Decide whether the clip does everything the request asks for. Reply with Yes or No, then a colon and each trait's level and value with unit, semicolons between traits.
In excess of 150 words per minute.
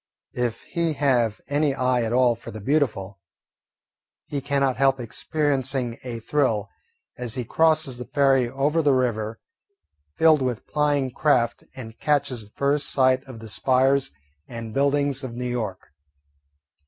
No: average, 145 wpm